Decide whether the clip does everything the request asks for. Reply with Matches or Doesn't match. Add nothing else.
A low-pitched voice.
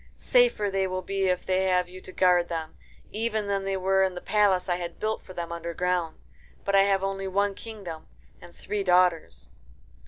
Doesn't match